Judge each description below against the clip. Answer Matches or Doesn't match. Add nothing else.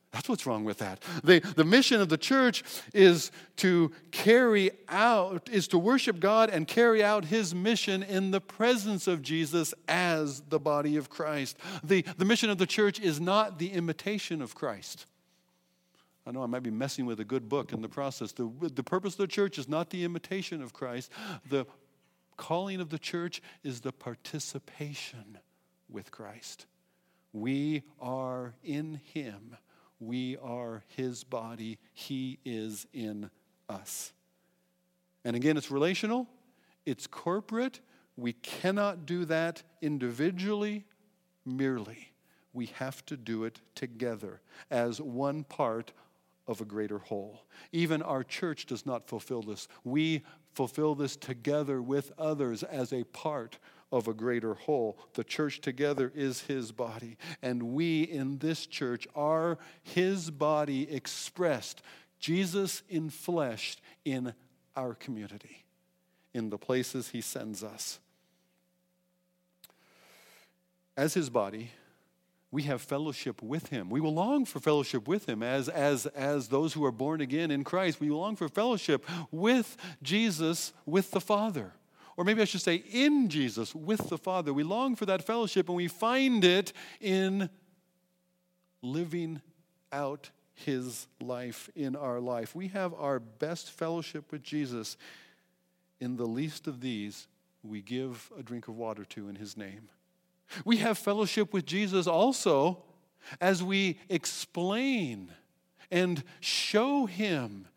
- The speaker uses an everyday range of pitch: Doesn't match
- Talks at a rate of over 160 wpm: Doesn't match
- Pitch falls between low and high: Matches